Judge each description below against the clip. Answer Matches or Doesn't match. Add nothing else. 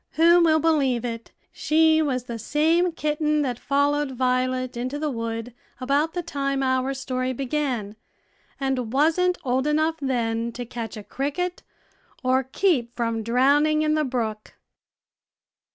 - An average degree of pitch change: Matches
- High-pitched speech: Matches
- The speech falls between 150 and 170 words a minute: Doesn't match